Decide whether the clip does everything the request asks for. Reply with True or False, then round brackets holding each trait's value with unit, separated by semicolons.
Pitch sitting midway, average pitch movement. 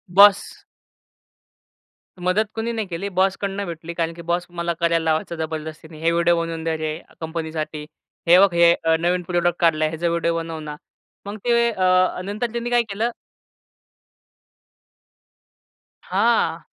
True (170 Hz; 3.1 semitones)